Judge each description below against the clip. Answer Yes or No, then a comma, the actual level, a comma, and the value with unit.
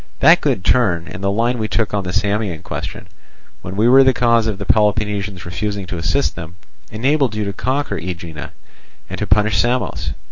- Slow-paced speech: No, average, 190 wpm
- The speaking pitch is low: Yes, low, 105 Hz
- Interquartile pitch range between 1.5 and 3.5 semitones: No, average, 4.1 semitones